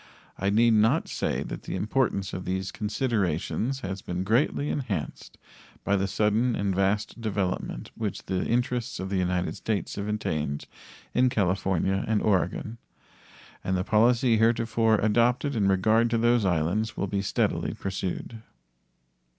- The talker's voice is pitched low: Yes, low, 105 Hz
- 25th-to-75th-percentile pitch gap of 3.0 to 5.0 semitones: Yes, average, 3.5 semitones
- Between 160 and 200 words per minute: No, average, 145 wpm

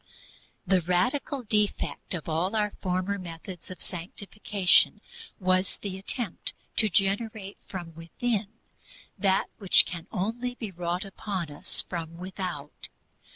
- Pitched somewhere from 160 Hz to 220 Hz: Yes, high, 190 Hz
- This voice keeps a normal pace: No, slow, 120 wpm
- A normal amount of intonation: Yes, average, 3.0 semitones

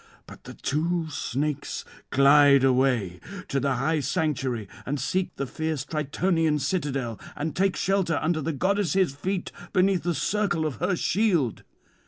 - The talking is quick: No, average, 150 wpm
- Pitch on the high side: No, medium, 155 Hz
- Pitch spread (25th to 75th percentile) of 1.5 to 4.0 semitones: No, average, 4.4 semitones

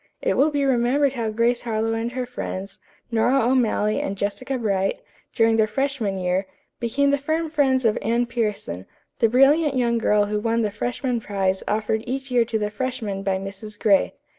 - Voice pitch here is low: No, high, 230 Hz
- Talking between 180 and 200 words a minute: Yes, average, 185 wpm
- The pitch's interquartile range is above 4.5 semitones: No, average, 3.7 semitones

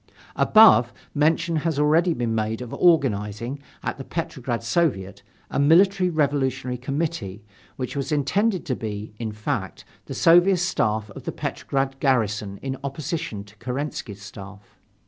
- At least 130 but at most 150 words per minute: Yes, average, 140 wpm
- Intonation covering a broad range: Yes, wide, 6.7 semitones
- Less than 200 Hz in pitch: Yes, low, 135 Hz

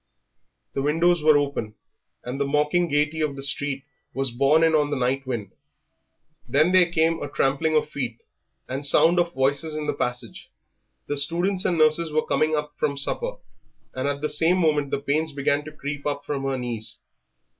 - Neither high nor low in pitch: Yes, medium, 145 Hz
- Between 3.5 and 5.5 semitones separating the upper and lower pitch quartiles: No, narrow, 2.4 semitones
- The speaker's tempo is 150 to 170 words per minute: No, average, 190 wpm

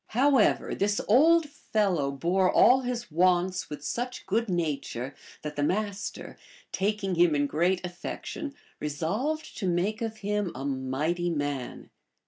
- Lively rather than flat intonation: Yes, wide, 6.3 semitones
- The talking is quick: No, slow, 135 wpm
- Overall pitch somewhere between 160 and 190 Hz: Yes, medium, 185 Hz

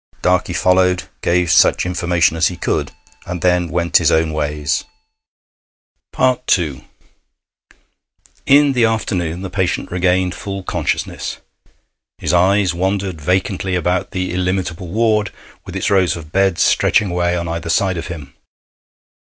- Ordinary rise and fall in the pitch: No, narrow, 1.9 semitones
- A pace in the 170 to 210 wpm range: No, slow, 135 wpm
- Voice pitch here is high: No, very low, 90 Hz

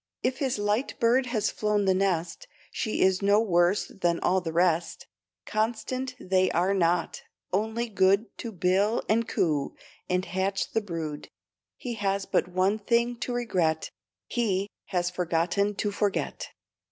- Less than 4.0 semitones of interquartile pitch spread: Yes, average, 3.5 semitones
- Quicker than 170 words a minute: No, average, 150 wpm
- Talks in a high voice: Yes, high, 195 Hz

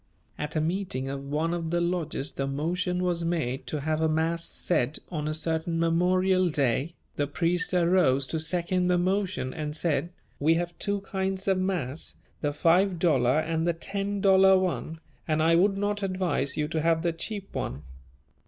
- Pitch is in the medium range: Yes, medium, 170 Hz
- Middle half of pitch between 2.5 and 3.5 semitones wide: Yes, average, 3.1 semitones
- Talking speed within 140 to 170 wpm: No, average, 180 wpm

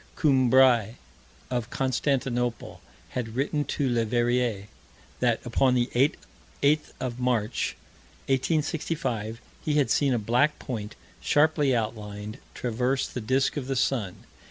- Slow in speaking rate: Yes, slow, 115 wpm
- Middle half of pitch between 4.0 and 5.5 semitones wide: No, average, 2.8 semitones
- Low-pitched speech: Yes, low, 125 Hz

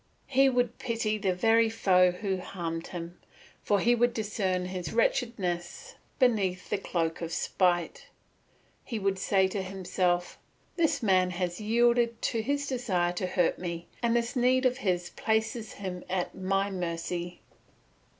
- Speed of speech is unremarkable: Yes, average, 150 wpm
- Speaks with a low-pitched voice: No, high, 195 Hz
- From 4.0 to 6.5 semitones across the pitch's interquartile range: Yes, average, 4.5 semitones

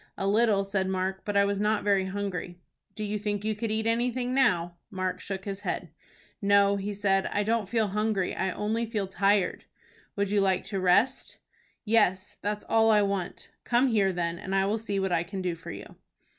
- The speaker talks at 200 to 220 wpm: Yes, fast, 205 wpm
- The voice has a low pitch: No, high, 200 Hz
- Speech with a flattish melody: Yes, narrow, 2.0 semitones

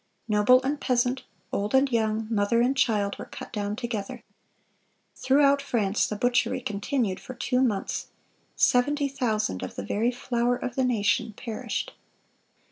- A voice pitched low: No, high, 240 Hz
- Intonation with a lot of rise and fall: No, average, 3.6 semitones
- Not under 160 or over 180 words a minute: No, average, 145 wpm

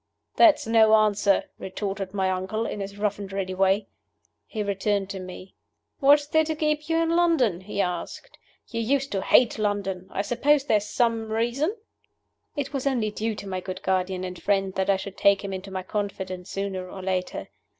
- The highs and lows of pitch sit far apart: No, average, 3.7 semitones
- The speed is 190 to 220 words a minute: Yes, average, 195 wpm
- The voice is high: Yes, high, 200 Hz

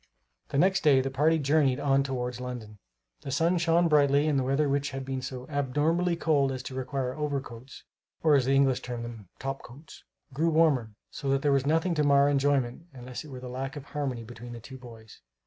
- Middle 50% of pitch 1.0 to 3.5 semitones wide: Yes, average, 2.8 semitones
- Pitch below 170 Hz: Yes, low, 135 Hz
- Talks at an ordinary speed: No, fast, 215 wpm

